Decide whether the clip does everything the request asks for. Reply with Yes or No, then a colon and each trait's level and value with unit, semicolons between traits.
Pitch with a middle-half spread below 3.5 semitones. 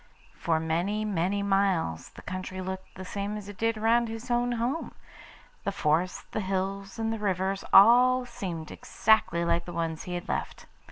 No: average, 3.8 semitones